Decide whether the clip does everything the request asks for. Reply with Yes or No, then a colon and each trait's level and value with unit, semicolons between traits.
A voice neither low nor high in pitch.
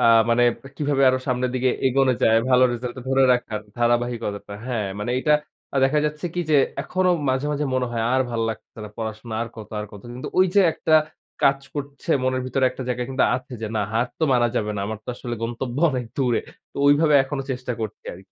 No: low, 125 Hz